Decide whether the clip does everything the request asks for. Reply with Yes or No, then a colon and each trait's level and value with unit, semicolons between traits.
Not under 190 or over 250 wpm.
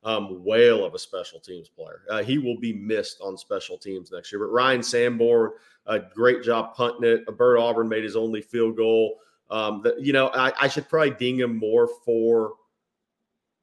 Yes: average, 200 wpm